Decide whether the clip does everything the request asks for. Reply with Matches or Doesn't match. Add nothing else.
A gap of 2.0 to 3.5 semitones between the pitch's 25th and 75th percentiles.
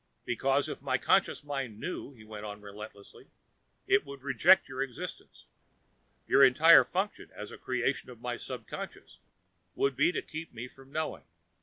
Doesn't match